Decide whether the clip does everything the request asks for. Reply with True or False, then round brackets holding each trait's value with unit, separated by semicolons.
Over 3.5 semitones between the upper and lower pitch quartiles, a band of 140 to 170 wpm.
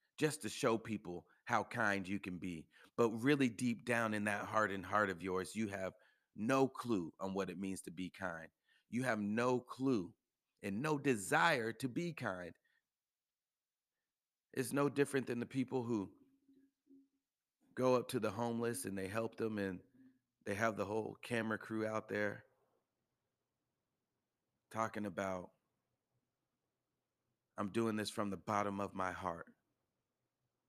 True (4.6 semitones; 150 wpm)